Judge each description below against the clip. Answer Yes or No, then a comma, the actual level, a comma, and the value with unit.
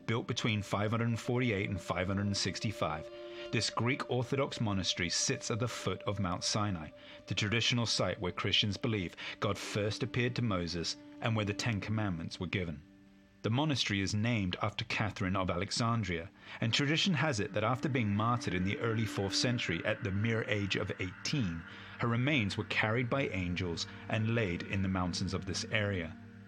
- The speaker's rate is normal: Yes, average, 170 wpm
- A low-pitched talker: Yes, low, 105 Hz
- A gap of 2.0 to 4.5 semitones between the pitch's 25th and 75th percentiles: Yes, average, 3.3 semitones